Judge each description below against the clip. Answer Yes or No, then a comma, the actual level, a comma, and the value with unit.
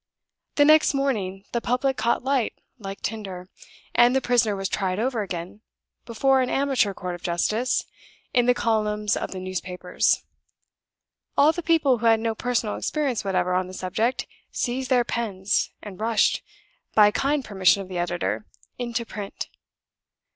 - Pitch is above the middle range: Yes, high, 220 Hz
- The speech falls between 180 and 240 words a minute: No, average, 155 wpm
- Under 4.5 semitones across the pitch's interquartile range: No, average, 4.8 semitones